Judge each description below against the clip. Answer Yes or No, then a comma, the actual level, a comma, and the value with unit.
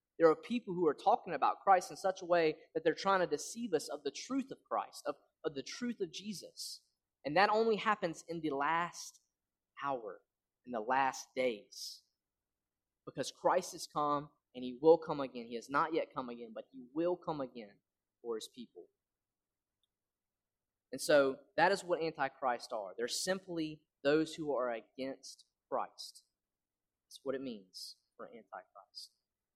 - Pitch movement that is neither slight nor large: No, wide, 6.2 semitones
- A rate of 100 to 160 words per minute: No, average, 170 wpm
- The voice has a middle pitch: Yes, medium, 165 Hz